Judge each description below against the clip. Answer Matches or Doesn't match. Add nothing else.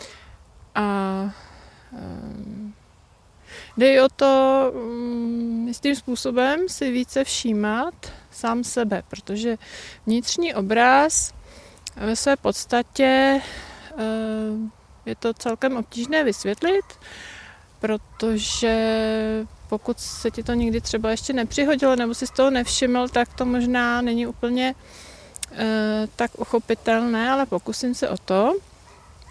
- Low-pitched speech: Doesn't match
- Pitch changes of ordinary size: Matches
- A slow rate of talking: Matches